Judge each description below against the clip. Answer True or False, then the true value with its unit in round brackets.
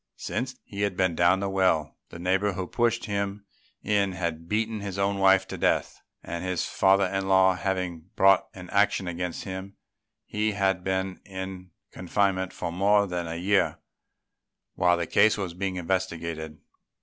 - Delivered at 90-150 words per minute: False (165 wpm)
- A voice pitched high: False (95 Hz)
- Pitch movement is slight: True (1.7 semitones)